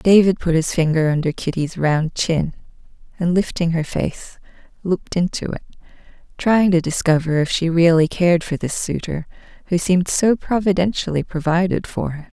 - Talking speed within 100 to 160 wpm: Yes, average, 155 wpm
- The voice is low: No, medium, 170 Hz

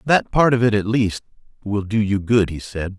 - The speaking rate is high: Yes, fast, 240 wpm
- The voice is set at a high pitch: No, low, 105 Hz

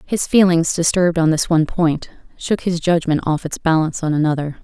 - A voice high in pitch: No, medium, 165 Hz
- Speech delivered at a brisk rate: No, average, 195 wpm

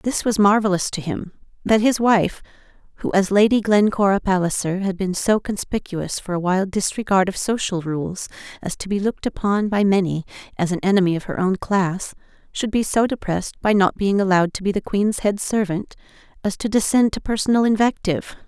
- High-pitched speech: Yes, high, 195 Hz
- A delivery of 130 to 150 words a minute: No, average, 185 wpm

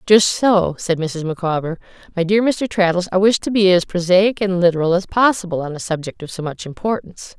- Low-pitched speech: No, medium, 185 Hz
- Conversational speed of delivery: No, fast, 210 wpm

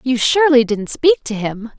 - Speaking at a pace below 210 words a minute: Yes, average, 200 wpm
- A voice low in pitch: No, very high, 255 Hz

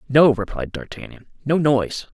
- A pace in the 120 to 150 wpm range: Yes, slow, 135 wpm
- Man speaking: Yes, male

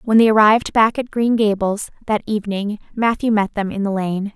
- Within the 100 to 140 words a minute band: No, fast, 205 wpm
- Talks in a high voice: Yes, high, 210 Hz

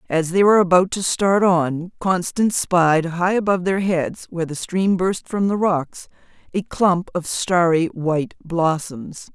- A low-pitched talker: No, medium, 175 Hz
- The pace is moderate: Yes, average, 165 wpm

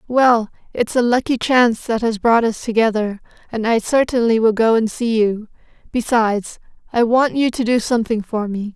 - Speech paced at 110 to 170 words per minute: No, average, 185 wpm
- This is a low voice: No, high, 230 Hz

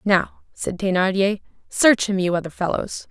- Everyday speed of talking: Yes, average, 155 wpm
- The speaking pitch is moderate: No, high, 195 Hz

